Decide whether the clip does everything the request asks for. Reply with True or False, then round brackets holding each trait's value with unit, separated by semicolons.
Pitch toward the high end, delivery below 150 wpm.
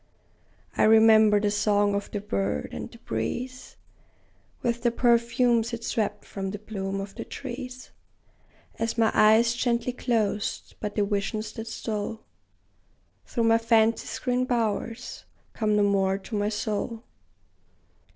True (220 Hz; 140 wpm)